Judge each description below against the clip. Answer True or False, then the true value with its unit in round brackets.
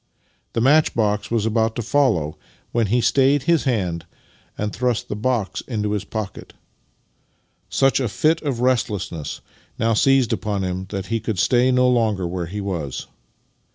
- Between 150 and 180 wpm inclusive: True (165 wpm)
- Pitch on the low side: True (110 Hz)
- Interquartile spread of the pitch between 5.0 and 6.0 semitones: False (4.2 semitones)